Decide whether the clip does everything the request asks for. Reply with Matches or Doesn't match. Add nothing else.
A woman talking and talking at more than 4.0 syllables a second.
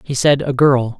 Doesn't match